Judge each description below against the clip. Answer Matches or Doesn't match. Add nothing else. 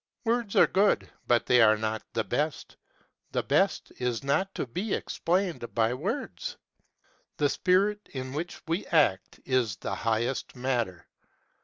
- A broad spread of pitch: Matches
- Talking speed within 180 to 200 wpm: Doesn't match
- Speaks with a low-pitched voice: Matches